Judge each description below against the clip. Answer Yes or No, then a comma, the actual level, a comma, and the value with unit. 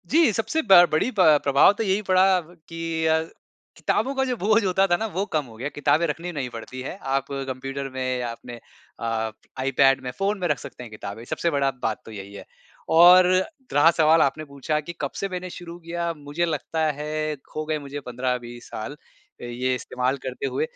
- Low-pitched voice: No, medium, 150 Hz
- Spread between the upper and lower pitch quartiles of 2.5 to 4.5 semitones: No, average, 5.3 semitones